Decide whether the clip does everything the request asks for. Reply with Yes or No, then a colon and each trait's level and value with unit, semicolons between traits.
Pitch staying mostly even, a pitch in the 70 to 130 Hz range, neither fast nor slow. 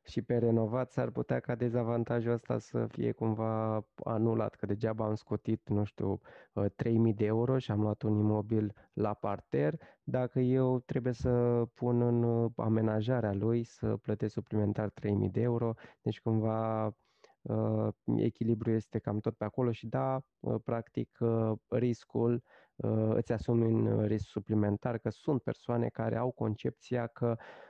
Yes: narrow, 1.8 semitones; low, 115 Hz; average, 145 wpm